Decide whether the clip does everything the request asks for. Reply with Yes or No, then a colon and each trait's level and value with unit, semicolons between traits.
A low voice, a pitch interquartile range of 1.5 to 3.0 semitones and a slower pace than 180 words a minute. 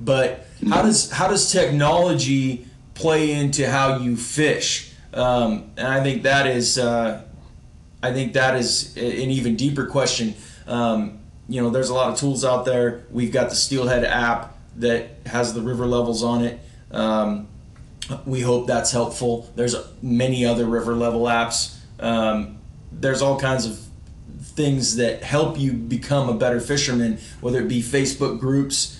Yes: low, 125 Hz; narrow, 2.4 semitones; average, 160 wpm